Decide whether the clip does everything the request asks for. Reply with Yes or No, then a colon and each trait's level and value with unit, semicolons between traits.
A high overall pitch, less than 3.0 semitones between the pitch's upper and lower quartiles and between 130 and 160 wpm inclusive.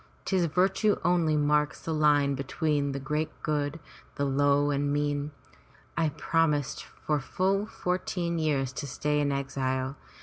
No: medium, 150 Hz; narrow, 2.5 semitones; average, 145 wpm